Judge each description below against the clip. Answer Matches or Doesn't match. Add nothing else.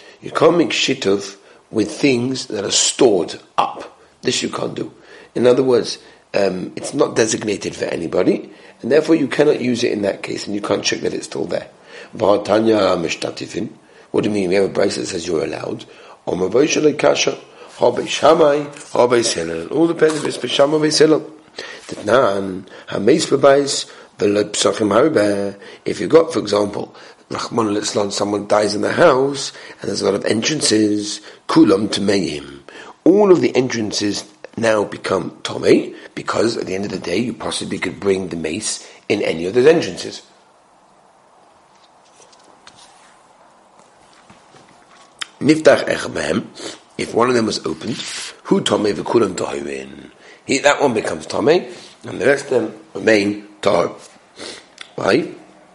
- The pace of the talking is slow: Matches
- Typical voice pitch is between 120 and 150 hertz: Doesn't match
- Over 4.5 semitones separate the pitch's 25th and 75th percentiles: Matches